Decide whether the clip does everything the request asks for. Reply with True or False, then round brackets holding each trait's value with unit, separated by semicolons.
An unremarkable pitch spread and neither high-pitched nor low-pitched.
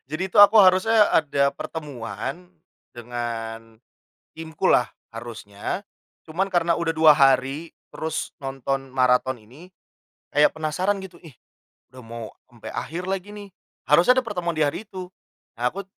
False (6.2 semitones; 155 Hz)